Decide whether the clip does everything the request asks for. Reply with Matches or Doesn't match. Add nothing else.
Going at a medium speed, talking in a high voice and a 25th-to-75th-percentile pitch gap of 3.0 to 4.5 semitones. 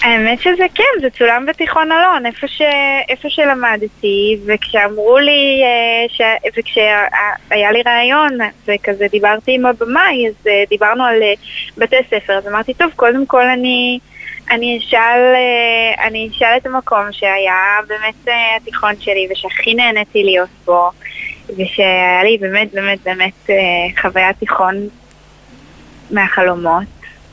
Matches